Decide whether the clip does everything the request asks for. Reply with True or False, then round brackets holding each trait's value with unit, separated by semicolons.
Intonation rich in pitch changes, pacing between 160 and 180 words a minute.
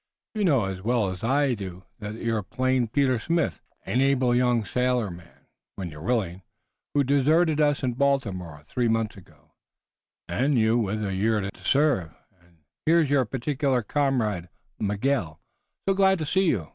True (5.9 semitones; 165 wpm)